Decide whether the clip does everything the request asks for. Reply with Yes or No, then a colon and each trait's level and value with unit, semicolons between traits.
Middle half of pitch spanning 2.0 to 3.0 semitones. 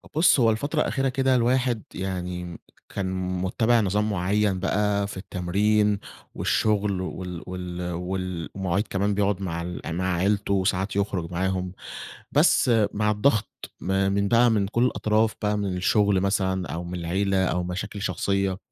Yes: narrow, 2.5 semitones